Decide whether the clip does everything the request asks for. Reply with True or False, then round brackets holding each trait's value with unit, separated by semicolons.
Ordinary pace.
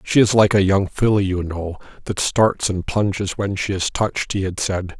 False (230 wpm)